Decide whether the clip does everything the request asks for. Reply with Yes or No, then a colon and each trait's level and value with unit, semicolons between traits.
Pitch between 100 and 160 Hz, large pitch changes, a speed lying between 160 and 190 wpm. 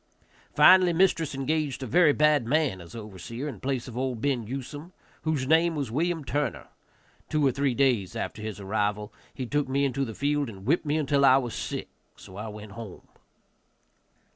No: low, 135 Hz; average, 4.7 semitones; average, 185 wpm